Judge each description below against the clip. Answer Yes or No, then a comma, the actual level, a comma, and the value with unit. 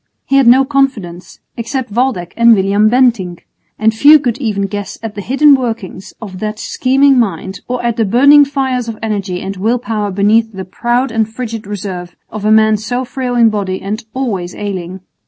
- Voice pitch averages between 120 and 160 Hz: No, high, 220 Hz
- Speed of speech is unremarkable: Yes, average, 190 wpm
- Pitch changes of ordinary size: Yes, average, 4.0 semitones